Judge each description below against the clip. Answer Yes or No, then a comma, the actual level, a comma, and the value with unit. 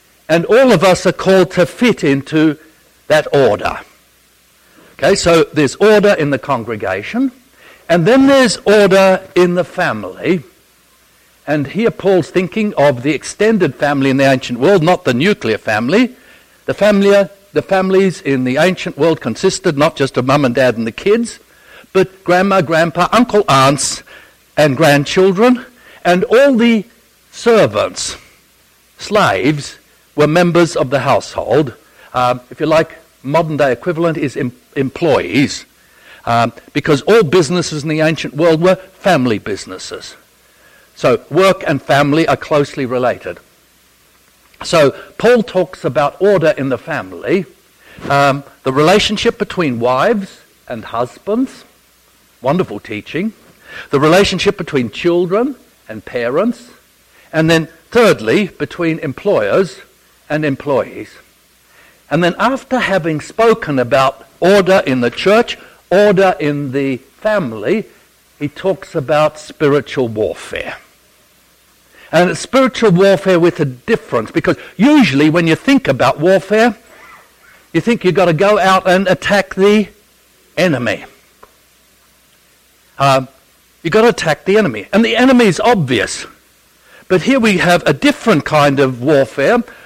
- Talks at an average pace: No, slow, 130 wpm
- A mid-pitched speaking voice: Yes, medium, 180 Hz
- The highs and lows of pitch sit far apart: Yes, wide, 6.0 semitones